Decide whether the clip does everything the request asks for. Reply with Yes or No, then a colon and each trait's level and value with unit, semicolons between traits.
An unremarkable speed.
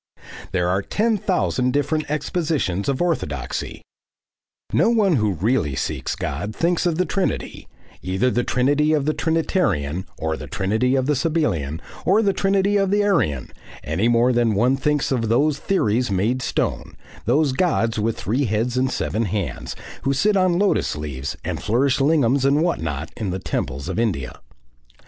Yes: average, 165 wpm